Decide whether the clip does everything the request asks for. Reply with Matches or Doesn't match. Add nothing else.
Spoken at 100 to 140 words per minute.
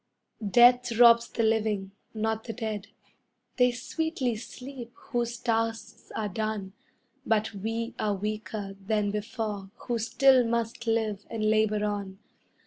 Matches